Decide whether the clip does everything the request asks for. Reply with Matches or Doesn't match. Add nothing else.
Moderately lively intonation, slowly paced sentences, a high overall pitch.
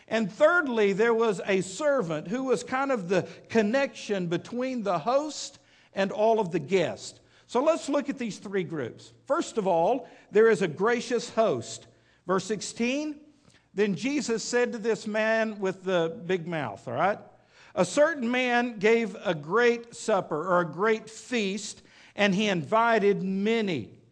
Doesn't match